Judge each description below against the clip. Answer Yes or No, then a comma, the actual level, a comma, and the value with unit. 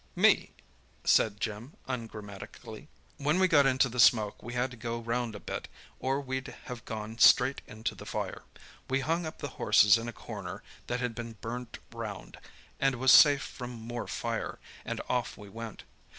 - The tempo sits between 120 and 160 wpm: No, average, 180 wpm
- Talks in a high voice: No, low, 120 Hz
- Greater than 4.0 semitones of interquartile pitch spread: No, average, 2.8 semitones